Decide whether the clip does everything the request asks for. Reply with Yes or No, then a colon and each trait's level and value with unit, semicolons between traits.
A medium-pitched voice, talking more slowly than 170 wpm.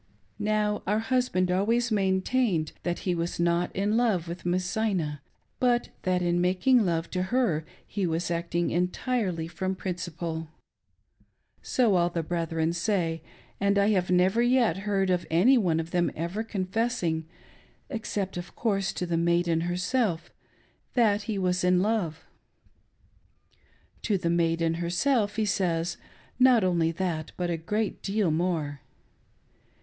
Yes: medium, 180 Hz; average, 145 wpm